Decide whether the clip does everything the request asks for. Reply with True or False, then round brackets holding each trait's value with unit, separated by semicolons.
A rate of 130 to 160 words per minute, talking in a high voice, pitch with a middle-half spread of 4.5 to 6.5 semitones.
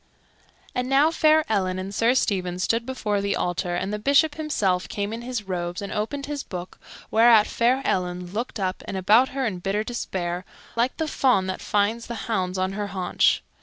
False (195 wpm; 210 Hz; 4.9 semitones)